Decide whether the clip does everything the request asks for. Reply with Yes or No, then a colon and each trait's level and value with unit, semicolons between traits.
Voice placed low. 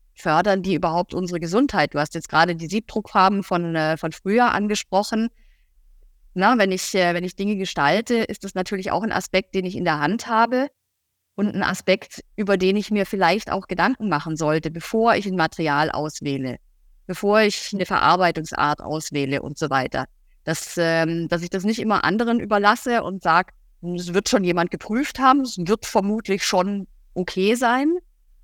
No: high, 190 Hz